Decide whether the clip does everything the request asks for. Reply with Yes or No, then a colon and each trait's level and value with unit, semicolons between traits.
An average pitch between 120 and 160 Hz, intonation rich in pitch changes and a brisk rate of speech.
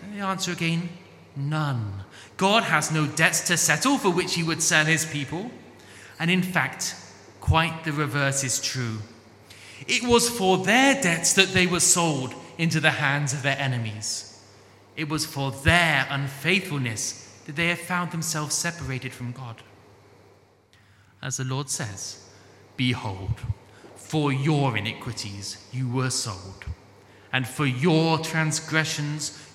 No: medium, 140 Hz; wide, 6.9 semitones; average, 140 wpm